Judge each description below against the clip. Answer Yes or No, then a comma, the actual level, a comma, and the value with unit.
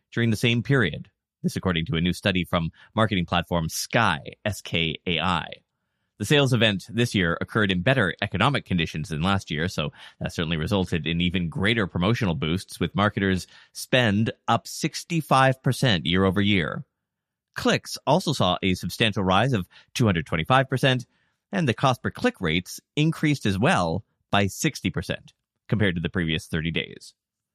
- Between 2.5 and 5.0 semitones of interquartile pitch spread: No, wide, 5.6 semitones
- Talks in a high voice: No, low, 100 Hz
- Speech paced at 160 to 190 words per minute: No, average, 150 wpm